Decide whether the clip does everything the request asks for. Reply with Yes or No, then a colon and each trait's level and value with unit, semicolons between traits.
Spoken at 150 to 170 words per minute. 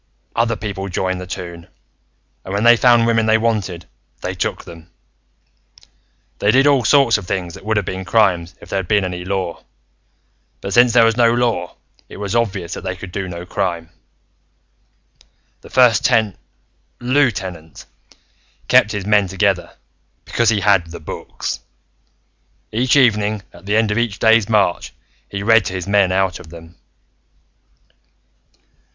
Yes: average, 160 wpm